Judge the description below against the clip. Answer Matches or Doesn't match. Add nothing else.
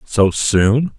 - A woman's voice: Doesn't match